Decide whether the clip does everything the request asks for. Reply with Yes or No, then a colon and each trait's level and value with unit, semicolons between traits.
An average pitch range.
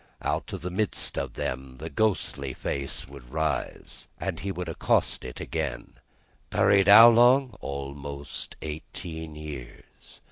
No: wide, 6.0 semitones